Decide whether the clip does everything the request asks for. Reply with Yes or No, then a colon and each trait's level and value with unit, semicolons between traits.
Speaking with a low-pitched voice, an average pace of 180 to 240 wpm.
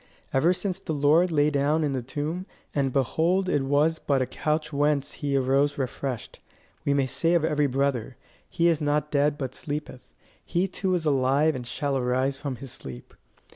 No: medium, 145 Hz; average, 185 wpm